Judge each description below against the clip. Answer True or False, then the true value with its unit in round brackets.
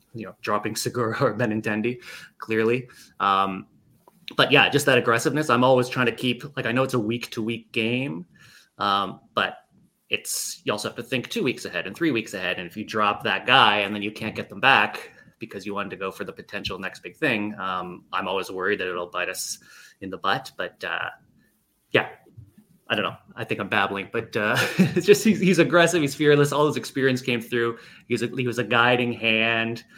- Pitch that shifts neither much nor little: True (3.3 semitones)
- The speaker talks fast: True (210 wpm)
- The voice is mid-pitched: False (120 Hz)